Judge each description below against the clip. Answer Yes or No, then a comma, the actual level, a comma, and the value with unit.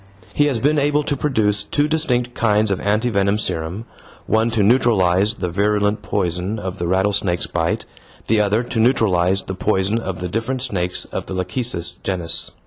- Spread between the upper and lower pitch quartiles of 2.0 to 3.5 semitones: No, average, 4.0 semitones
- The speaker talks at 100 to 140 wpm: No, average, 175 wpm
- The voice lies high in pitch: No, low, 105 Hz